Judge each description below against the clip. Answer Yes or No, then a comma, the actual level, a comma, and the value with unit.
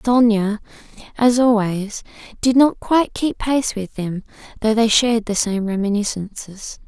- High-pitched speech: Yes, high, 220 Hz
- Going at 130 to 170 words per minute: Yes, average, 140 wpm